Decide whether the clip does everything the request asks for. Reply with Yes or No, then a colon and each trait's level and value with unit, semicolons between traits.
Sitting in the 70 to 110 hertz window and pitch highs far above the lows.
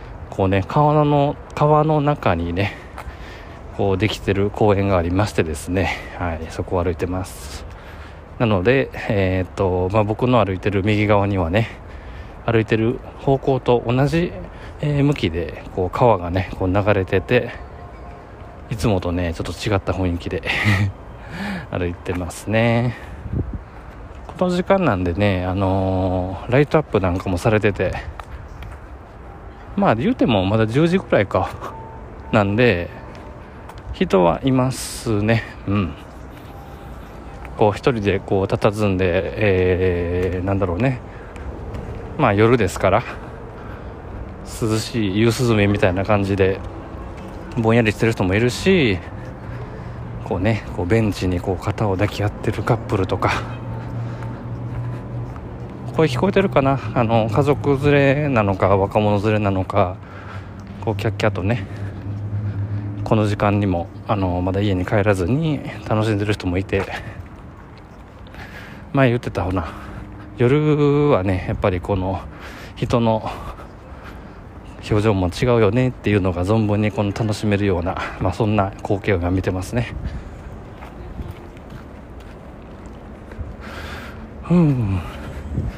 No: low, 100 Hz; average, 3.7 semitones